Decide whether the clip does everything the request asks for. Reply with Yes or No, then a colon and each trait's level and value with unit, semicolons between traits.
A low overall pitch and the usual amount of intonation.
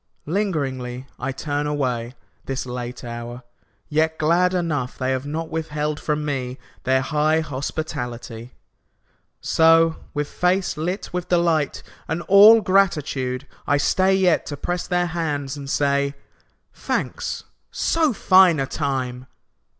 No: medium, 150 Hz; average, 4.5 semitones